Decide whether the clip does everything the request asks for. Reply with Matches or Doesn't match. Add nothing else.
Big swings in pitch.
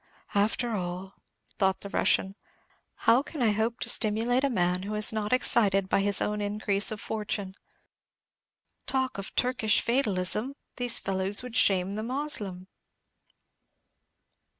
Doesn't match